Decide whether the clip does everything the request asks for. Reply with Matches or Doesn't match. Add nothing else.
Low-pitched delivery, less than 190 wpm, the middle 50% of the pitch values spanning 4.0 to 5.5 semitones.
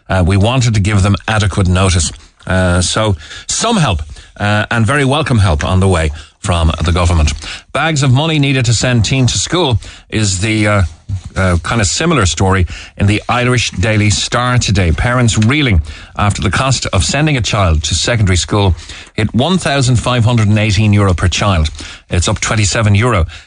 Matches